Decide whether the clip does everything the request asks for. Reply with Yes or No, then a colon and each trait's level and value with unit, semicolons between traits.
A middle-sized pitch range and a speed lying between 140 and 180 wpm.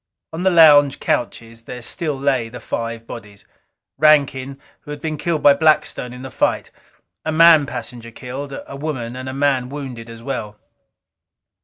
Yes: average, 3.8 semitones; average, 165 wpm